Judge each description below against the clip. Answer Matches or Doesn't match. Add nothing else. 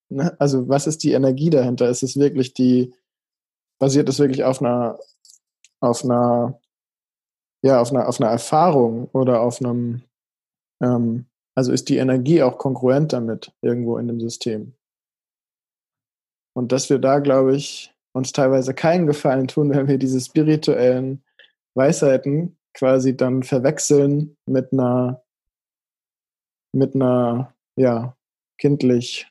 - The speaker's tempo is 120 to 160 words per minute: Matches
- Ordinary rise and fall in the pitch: Doesn't match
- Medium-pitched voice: Doesn't match